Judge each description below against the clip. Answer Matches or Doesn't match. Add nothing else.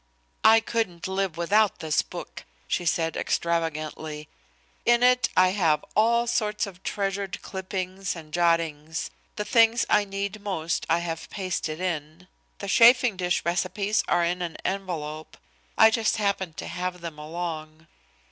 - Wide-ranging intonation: Doesn't match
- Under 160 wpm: Matches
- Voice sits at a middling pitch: Matches